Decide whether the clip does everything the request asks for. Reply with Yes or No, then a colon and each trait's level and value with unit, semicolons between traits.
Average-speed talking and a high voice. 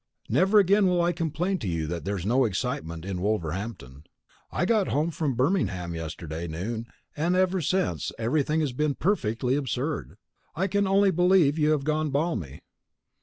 No: average, 170 wpm; low, 135 Hz